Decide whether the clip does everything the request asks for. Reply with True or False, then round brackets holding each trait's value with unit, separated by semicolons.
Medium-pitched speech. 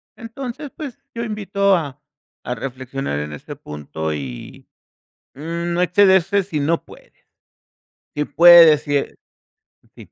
True (170 Hz)